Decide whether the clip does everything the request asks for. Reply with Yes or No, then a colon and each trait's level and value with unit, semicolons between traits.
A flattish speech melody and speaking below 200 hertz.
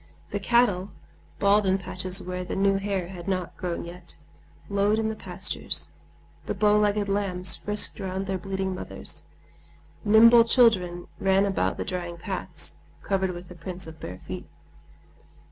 Yes: narrow, 2.1 semitones; high, 190 Hz